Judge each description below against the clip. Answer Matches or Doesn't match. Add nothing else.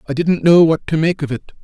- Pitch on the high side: Doesn't match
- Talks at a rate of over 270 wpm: Matches